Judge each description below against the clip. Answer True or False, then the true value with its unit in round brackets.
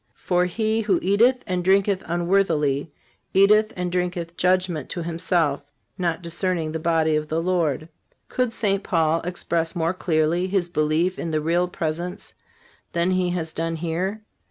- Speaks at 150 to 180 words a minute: True (155 wpm)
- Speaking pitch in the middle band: True (175 Hz)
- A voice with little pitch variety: True (2.3 semitones)